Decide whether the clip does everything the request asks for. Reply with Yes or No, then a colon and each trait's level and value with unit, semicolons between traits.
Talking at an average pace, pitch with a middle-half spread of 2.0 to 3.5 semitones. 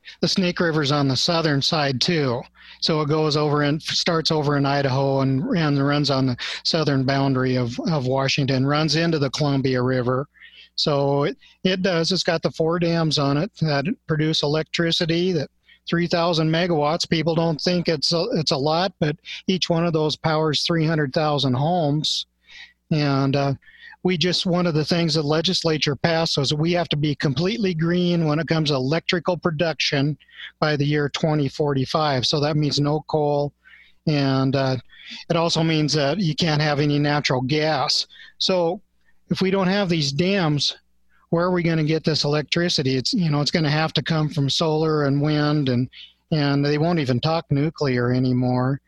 Yes: average, 180 wpm; average, 3.0 semitones